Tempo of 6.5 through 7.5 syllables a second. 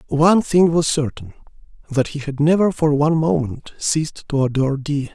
No: 5.4 syllables/s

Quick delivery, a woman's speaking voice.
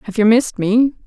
Yes: fast, 225 wpm; female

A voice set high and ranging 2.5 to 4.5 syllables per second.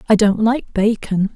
Yes: high, 215 Hz; 4.3 syllables/s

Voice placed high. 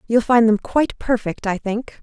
Yes: high, 225 Hz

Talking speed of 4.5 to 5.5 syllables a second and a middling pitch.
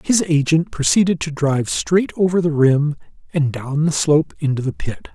Yes: 5.0 syllables/s; medium, 150 Hz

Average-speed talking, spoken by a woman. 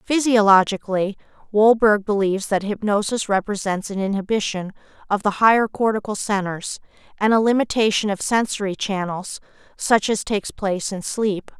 No: slow, 130 wpm; female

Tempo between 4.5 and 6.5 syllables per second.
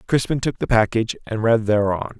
Yes: 5.6 syllables/s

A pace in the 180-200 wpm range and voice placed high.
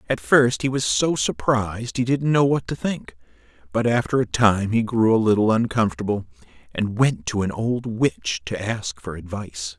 No: average, 190 wpm; low, 110 Hz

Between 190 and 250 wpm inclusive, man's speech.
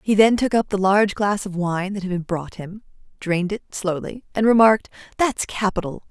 No: fast, 205 wpm; female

